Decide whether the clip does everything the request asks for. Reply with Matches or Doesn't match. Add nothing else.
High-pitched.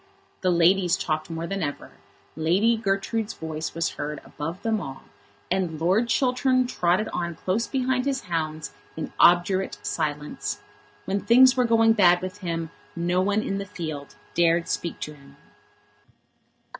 Doesn't match